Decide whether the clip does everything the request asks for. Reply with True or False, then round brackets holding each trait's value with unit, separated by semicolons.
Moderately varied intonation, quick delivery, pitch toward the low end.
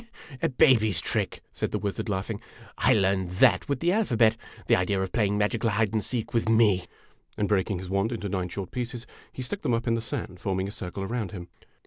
True (3.4 semitones; 220 wpm; 105 Hz)